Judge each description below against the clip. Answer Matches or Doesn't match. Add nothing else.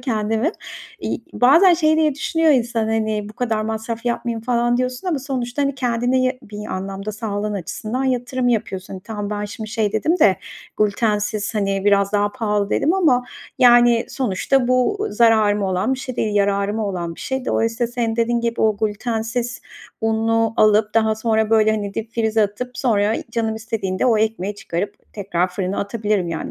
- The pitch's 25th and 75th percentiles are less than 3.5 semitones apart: Matches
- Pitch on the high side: Matches